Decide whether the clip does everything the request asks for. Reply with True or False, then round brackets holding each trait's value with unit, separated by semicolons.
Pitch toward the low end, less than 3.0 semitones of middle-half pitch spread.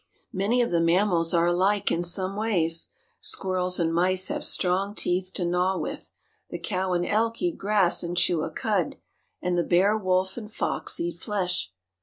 False (185 Hz; 2.4 semitones)